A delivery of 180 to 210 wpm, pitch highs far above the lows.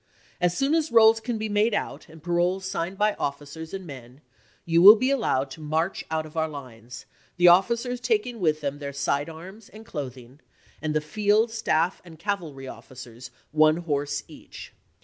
Yes: average, 185 wpm; wide, 6.4 semitones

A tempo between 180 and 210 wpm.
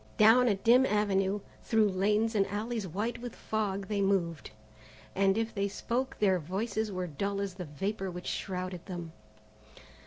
No: average, 160 wpm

